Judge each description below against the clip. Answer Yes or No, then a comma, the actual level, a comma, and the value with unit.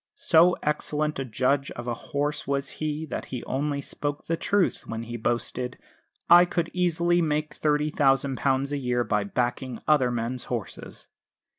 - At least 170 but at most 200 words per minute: No, average, 155 wpm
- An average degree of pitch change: Yes, average, 3.7 semitones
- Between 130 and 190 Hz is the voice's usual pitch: Yes, medium, 140 Hz